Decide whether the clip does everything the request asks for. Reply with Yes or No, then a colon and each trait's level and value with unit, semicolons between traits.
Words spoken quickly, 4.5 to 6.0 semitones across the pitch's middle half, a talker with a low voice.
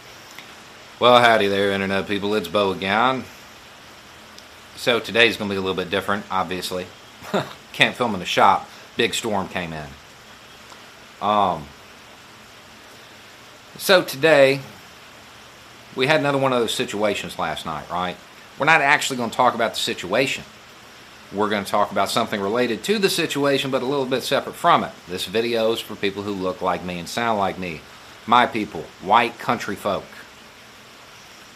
No: average, 160 wpm; average, 4.9 semitones; low, 100 Hz